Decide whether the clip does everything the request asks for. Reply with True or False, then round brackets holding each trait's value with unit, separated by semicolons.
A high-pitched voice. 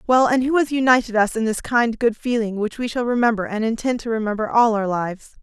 True (230 Hz)